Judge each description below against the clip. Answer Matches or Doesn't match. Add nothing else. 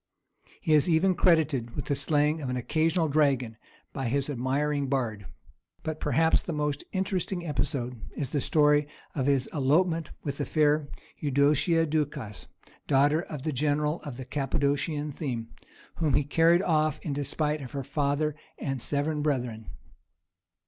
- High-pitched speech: Doesn't match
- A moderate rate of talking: Matches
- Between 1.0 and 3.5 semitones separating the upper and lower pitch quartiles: Matches